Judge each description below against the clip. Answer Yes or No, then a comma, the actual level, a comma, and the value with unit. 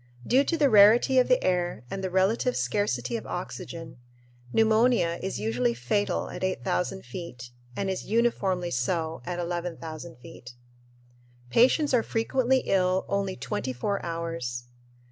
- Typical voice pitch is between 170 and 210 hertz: Yes, medium, 185 Hz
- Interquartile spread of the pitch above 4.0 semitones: Yes, wide, 5.4 semitones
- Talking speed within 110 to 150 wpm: Yes, slow, 135 wpm